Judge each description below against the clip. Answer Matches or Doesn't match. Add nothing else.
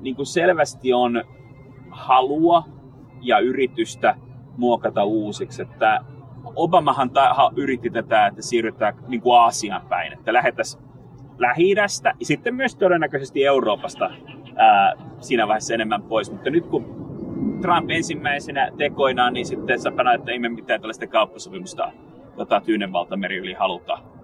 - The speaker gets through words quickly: Doesn't match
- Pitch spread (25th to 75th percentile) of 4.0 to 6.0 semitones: Matches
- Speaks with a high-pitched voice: Doesn't match